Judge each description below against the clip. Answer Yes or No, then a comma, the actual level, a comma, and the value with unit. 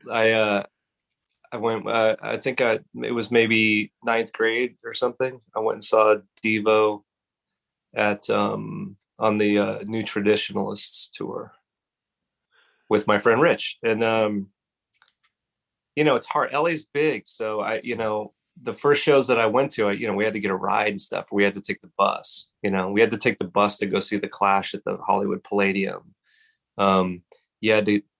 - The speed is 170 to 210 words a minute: Yes, average, 190 wpm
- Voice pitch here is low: Yes, low, 110 Hz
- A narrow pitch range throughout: Yes, narrow, 1.9 semitones